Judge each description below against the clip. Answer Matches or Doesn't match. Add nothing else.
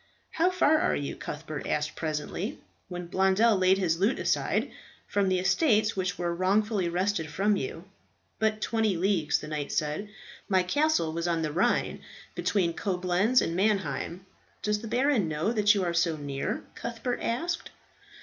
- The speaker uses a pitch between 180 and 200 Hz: Matches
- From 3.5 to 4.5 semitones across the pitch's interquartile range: Matches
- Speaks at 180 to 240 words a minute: Doesn't match